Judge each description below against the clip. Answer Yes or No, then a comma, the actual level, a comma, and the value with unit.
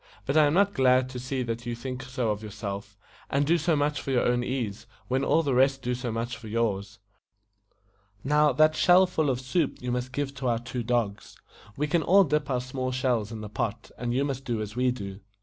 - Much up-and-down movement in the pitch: No, average, 3.3 semitones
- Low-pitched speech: Yes, low, 125 Hz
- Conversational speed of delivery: No, fast, 235 wpm